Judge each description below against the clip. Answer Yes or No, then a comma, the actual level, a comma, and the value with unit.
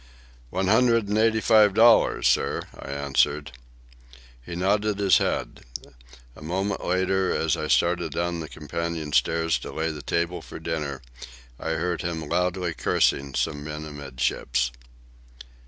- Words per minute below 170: Yes, average, 140 wpm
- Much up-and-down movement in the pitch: No, average, 4.0 semitones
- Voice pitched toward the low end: Yes, very low, 85 Hz